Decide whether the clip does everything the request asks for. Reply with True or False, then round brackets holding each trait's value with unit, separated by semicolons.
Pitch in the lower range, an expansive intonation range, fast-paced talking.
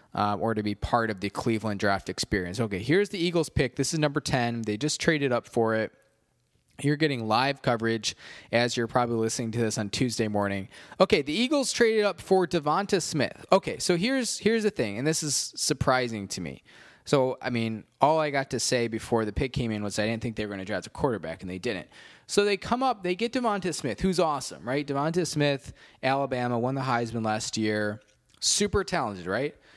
True (125 Hz; 6.4 semitones; 215 wpm)